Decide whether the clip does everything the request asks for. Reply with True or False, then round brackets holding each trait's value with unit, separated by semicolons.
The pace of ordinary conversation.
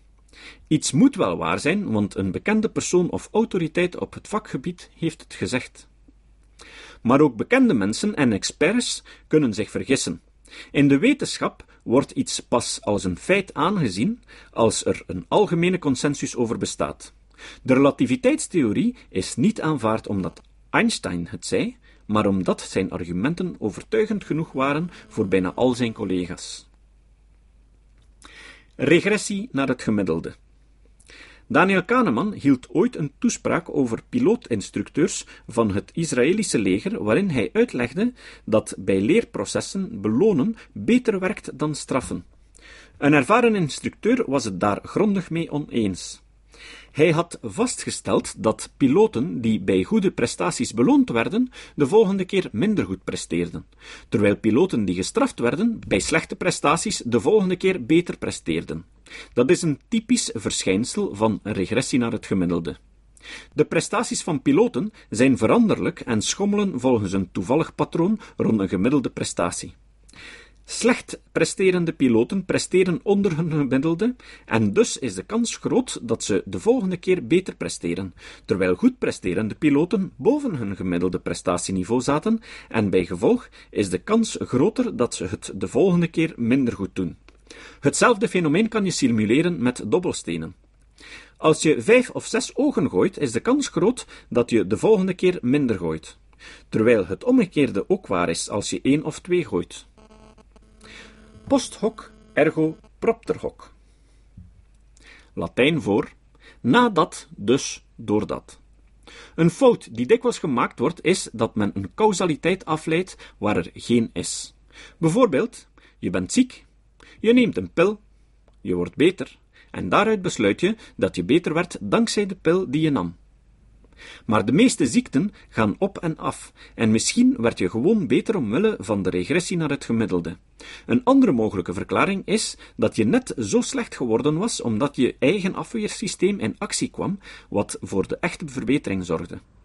True (145 wpm)